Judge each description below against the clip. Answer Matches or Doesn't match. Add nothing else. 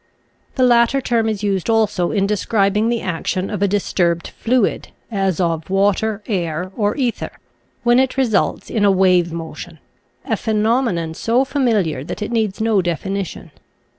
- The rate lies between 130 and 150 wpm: Doesn't match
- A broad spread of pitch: Doesn't match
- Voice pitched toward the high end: Matches